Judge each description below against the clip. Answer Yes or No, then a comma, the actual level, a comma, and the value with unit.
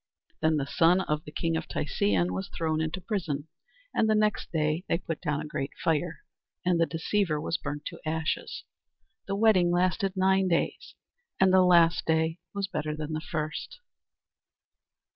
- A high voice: No, medium, 165 Hz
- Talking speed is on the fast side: No, average, 170 wpm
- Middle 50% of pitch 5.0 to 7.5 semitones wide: No, average, 3.2 semitones